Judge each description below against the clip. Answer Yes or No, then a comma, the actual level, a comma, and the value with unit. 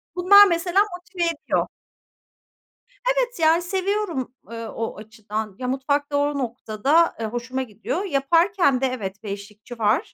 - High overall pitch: Yes, very high, 270 Hz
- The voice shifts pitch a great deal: Yes, wide, 7.5 semitones